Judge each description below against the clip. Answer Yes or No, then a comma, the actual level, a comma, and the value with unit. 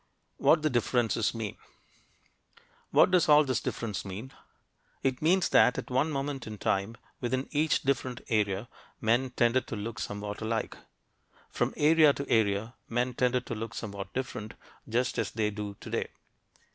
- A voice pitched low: Yes, low, 120 Hz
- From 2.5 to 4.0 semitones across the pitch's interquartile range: Yes, average, 3.7 semitones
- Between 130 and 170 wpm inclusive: Yes, average, 155 wpm